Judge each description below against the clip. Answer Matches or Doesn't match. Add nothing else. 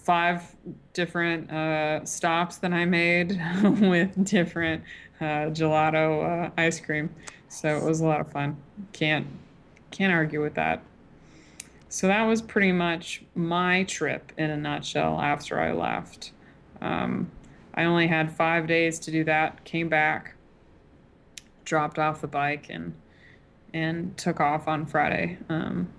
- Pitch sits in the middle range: Matches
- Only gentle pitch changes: Matches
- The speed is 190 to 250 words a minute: Doesn't match